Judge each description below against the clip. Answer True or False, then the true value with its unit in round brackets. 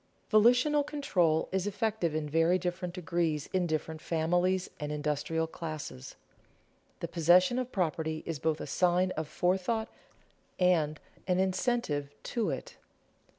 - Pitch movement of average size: True (3.1 semitones)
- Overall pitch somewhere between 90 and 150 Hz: False (175 Hz)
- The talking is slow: True (130 wpm)